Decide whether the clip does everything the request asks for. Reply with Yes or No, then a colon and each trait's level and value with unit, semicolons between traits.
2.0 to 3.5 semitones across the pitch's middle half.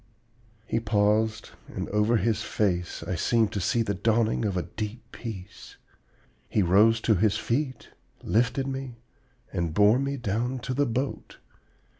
Yes: average, 2.7 semitones